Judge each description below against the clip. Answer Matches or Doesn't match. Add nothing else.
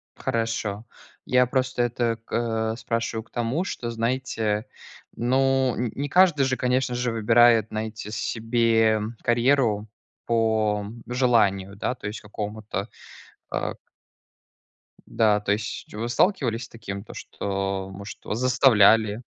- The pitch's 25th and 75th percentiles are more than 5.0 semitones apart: Doesn't match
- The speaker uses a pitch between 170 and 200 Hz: Doesn't match